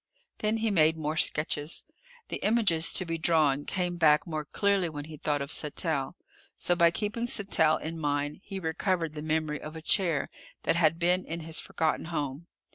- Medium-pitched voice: Yes, medium, 160 Hz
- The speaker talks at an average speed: Yes, average, 185 wpm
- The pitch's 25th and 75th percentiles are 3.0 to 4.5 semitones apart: No, narrow, 2.6 semitones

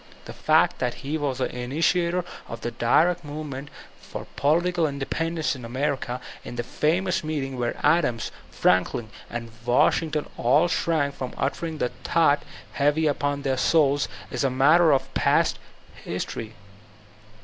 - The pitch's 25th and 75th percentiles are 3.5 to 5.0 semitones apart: Yes, average, 3.9 semitones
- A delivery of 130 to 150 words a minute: Yes, average, 140 wpm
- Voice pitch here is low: No, medium, 145 Hz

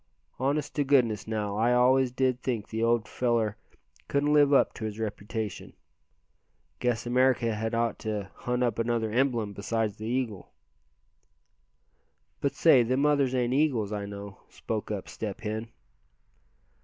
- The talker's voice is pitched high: No, low, 115 Hz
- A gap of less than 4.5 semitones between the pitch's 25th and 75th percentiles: Yes, average, 3.0 semitones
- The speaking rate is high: No, average, 145 wpm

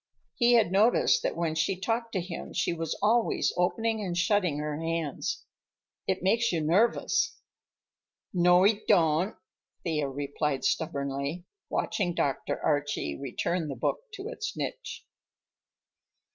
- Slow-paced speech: Yes, slow, 130 wpm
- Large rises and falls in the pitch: Yes, wide, 6.1 semitones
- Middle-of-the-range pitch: Yes, medium, 175 Hz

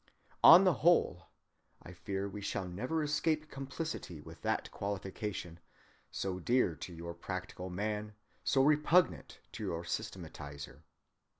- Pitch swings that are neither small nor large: No, wide, 7.7 semitones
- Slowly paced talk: Yes, slow, 120 wpm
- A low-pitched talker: Yes, low, 100 Hz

